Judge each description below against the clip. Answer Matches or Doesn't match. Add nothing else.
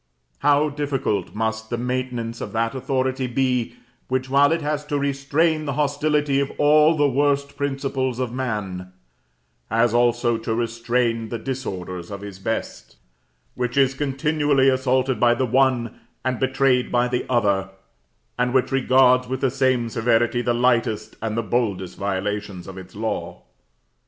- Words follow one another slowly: Doesn't match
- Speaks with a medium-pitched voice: Doesn't match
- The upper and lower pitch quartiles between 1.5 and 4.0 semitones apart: Matches